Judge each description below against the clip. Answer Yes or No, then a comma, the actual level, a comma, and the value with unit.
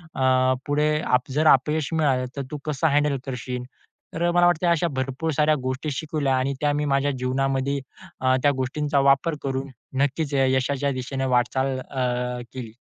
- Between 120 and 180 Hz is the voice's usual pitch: Yes, low, 135 Hz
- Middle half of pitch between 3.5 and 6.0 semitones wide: No, narrow, 2.4 semitones